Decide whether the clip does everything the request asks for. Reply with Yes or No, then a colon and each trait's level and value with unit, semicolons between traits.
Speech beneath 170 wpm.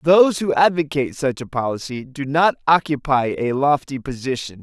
Yes: average, 155 wpm